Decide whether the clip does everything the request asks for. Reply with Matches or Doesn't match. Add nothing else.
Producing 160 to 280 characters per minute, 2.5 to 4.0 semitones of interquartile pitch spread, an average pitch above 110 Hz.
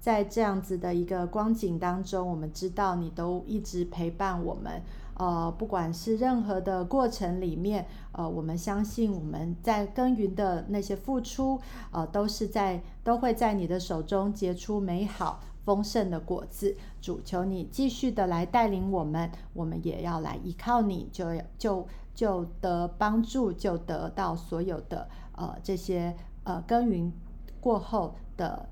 Matches